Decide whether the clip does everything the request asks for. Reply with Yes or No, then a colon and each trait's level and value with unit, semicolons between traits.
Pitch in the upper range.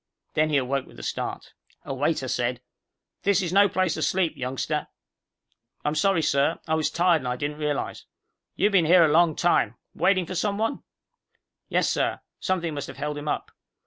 No: medium, 155 Hz